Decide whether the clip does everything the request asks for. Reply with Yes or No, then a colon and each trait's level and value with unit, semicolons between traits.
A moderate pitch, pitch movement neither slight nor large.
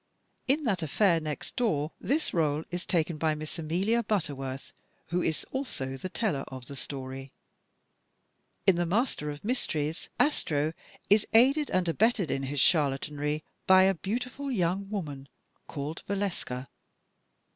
No: medium, 165 Hz; wide, 5.9 semitones